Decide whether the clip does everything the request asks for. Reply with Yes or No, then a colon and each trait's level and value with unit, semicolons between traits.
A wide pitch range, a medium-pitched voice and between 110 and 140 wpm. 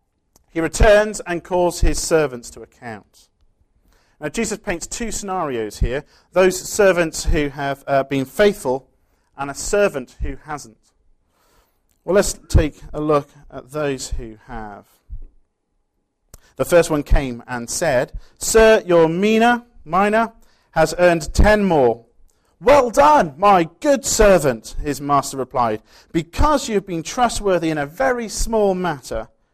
Yes: wide, 6.9 semitones; medium, 165 Hz; slow, 135 wpm